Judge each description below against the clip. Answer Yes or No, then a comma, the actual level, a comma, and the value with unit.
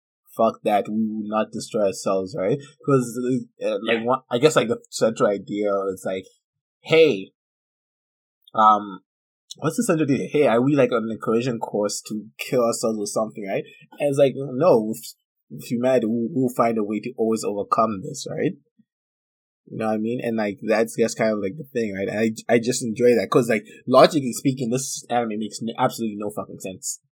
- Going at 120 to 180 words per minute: No, average, 200 wpm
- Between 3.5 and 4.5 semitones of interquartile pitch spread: No, average, 3.1 semitones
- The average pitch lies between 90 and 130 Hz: Yes, low, 115 Hz